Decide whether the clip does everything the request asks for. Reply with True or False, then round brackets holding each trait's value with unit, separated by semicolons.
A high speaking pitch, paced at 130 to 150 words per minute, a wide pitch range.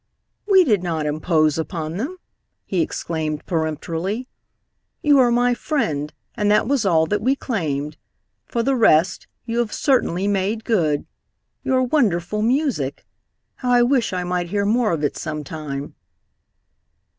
True (195 Hz; 145 wpm; 7.3 semitones)